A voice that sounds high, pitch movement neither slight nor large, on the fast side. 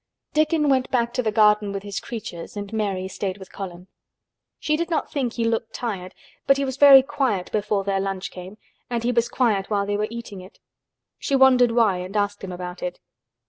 Yes: high, 210 Hz; average, 4.2 semitones; fast, 210 wpm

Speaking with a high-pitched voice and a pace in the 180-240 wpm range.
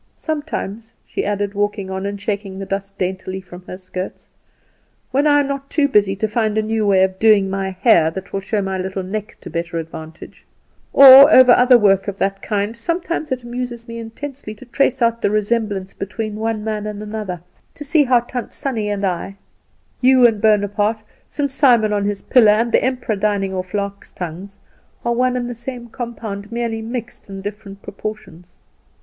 Yes: high, 210 Hz; average, 190 wpm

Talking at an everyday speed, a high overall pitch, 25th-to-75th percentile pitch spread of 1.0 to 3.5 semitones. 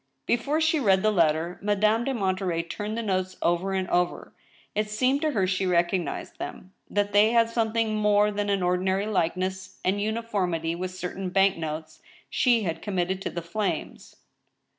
Yes: average, 170 wpm; high, 195 Hz; average, 3.1 semitones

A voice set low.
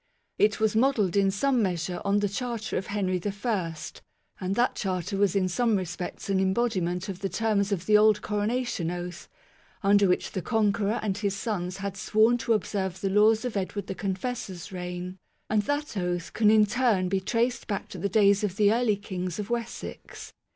No: high, 200 Hz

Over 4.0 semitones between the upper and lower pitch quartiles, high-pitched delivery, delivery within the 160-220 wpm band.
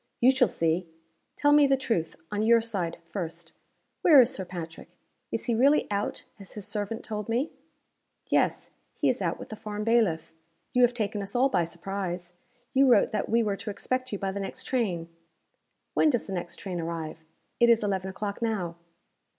Yes: average, 4.9 semitones; high, 205 Hz; average, 190 wpm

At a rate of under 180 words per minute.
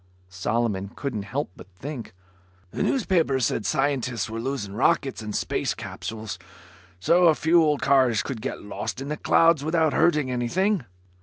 Yes: average, 155 wpm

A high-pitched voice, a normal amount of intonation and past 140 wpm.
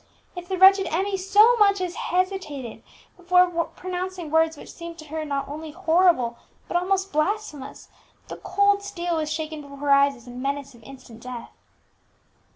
Yes: very high, 335 Hz; average, 4.8 semitones; average, 165 wpm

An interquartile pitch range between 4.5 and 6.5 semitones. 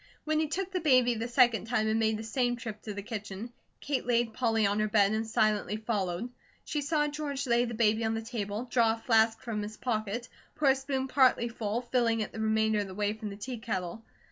No: narrow, 2.5 semitones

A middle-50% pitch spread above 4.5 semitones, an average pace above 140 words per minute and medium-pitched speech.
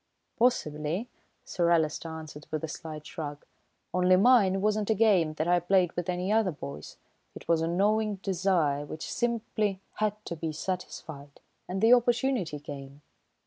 Yes: average, 5.1 semitones; average, 155 wpm; medium, 180 Hz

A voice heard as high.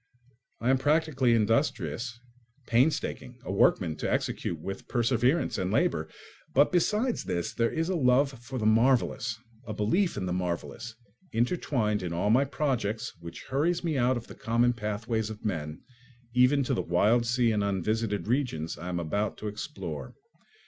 No: low, 115 Hz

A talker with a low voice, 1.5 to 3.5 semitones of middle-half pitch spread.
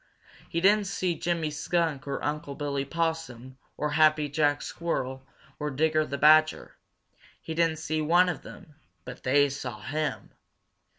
No: medium, 155 Hz; narrow, 2.5 semitones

